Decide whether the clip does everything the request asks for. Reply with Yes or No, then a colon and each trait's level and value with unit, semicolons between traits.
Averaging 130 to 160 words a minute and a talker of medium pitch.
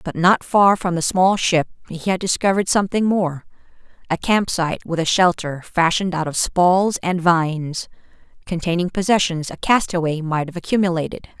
Yes: average, 155 wpm; medium, 175 Hz